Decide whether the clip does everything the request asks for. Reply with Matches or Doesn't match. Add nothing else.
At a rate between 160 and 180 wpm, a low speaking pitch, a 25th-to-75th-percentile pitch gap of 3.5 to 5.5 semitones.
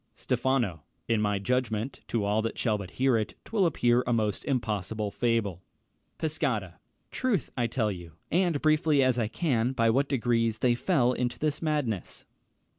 Matches